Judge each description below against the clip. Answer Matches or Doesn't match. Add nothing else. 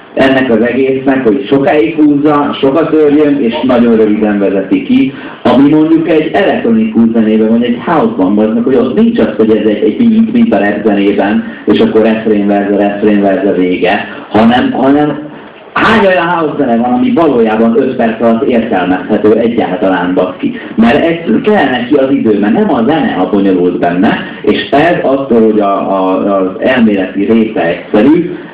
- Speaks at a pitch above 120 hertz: Doesn't match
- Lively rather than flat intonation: Matches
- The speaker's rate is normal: Doesn't match